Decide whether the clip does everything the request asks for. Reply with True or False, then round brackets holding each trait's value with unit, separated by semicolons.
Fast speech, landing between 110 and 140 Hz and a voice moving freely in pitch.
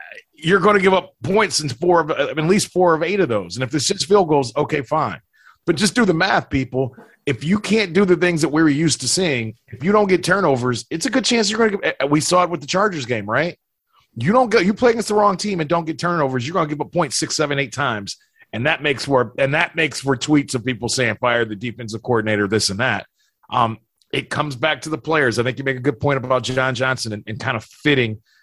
False (265 wpm; 150 Hz; 6.1 semitones)